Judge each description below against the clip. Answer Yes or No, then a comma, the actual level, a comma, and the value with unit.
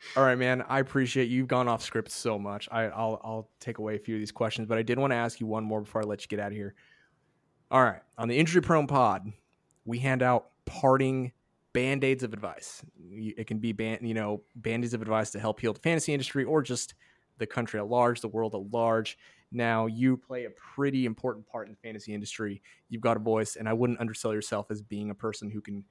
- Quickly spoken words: Yes, fast, 245 wpm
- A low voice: Yes, low, 115 Hz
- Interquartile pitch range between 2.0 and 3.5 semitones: Yes, narrow, 2.6 semitones